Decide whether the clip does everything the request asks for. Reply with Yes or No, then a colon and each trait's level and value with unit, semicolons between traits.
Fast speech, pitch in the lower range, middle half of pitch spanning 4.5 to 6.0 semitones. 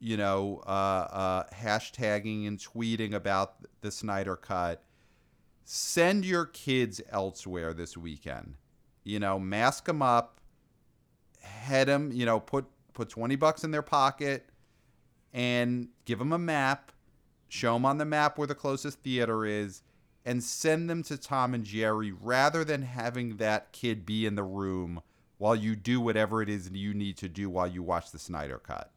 No: average, 165 wpm; low, 110 Hz; wide, 5.4 semitones